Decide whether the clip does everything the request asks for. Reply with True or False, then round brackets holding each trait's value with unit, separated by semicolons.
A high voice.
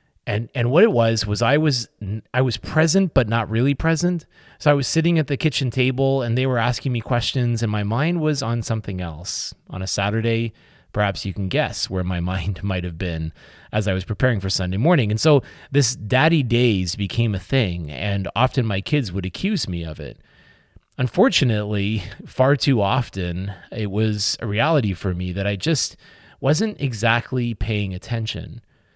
False (115 Hz)